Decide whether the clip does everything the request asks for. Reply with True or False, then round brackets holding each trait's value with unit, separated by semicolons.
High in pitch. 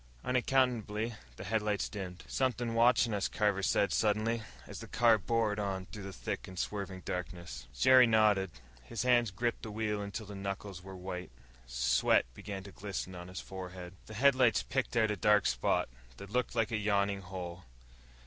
False (105 Hz)